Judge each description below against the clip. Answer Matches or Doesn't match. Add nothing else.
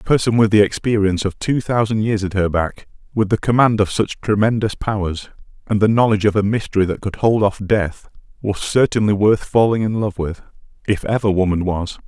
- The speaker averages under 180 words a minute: Doesn't match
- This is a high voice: Doesn't match